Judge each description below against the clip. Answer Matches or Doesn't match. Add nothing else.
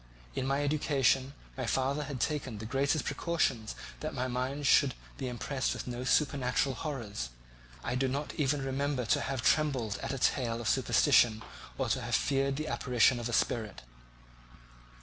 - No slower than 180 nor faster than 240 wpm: Doesn't match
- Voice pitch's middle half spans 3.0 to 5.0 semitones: Doesn't match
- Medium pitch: Doesn't match